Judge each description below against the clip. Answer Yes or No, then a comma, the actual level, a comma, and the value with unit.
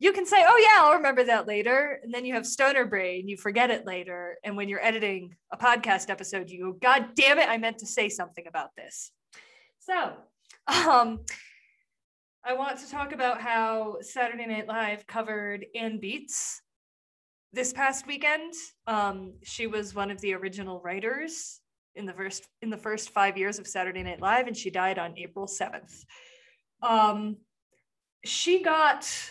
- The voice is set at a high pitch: Yes, high, 225 Hz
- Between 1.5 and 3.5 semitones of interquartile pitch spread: No, wide, 5.4 semitones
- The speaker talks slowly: No, average, 170 wpm